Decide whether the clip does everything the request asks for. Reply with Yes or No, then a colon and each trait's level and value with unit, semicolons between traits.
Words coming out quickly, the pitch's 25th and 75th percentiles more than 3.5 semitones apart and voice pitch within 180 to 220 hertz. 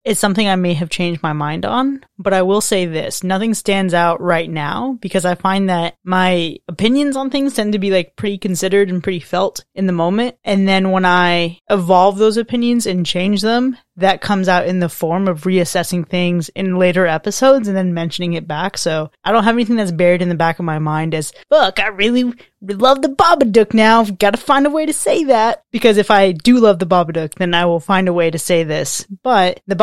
Yes: fast, 230 wpm; average, 3.9 semitones; high, 190 Hz